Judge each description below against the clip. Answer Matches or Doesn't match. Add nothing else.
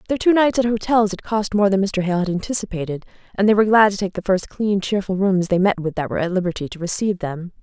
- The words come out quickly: Matches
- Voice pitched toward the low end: Doesn't match